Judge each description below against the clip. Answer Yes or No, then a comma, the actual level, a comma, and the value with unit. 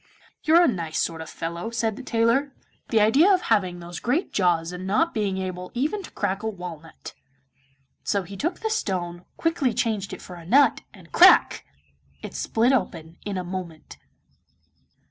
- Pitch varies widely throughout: Yes, wide, 6.1 semitones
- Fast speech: No, average, 175 wpm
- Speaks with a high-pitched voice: Yes, high, 200 Hz